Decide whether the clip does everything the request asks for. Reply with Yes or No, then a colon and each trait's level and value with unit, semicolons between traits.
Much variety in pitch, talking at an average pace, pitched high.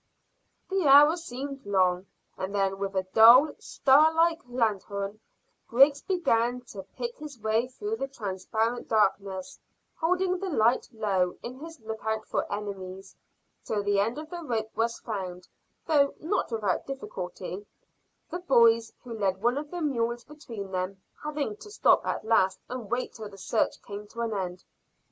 Yes: wide, 6.0 semitones; average, 160 wpm; high, 230 Hz